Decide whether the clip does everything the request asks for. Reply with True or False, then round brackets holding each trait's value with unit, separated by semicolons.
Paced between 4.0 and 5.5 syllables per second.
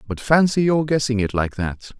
True (4.9 syllables/s)